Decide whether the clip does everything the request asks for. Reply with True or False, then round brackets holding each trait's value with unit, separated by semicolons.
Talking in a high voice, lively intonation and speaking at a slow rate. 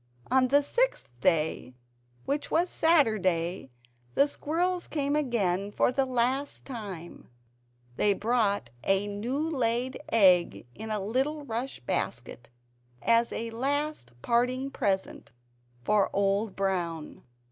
True (230 Hz; 6.0 semitones; 115 wpm)